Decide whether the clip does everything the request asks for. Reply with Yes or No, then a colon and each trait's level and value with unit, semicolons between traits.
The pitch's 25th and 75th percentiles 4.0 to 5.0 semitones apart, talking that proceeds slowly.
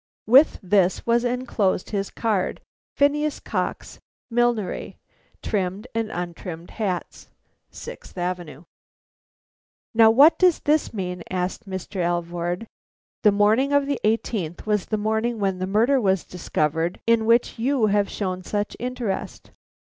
Yes: average, 4.4 semitones; slow, 130 wpm